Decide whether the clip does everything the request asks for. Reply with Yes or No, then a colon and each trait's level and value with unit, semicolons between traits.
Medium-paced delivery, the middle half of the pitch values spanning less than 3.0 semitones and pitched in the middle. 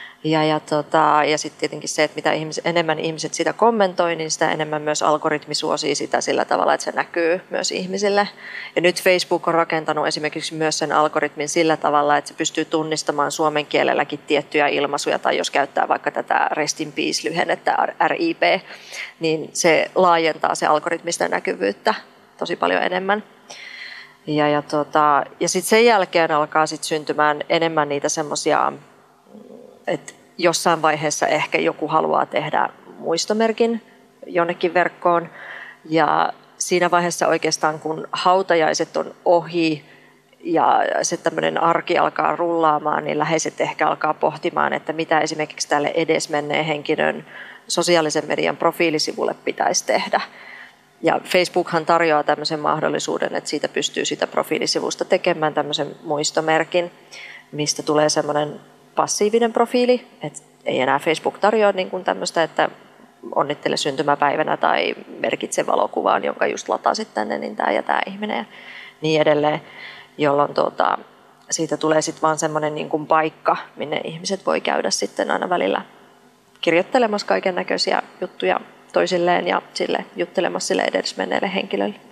Yes: average, 140 wpm; narrow, 2.5 semitones; medium, 160 Hz